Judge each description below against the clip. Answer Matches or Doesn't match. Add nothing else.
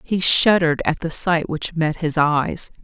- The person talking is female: Matches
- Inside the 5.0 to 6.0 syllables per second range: Doesn't match